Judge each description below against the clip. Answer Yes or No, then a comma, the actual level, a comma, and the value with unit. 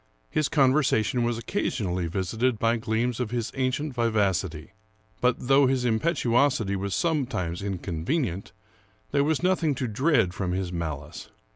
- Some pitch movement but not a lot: No, wide, 5.7 semitones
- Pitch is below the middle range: Yes, low, 115 Hz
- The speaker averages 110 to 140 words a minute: Yes, slow, 135 wpm